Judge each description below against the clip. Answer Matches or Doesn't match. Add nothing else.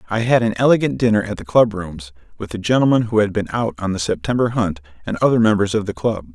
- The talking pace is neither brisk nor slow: Doesn't match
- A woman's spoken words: Doesn't match